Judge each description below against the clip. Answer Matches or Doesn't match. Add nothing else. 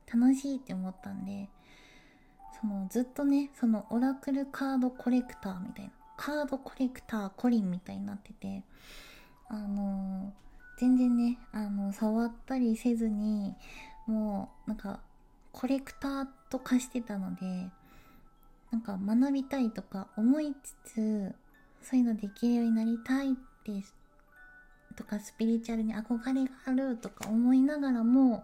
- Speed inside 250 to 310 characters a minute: Matches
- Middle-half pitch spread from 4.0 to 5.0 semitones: Matches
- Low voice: Doesn't match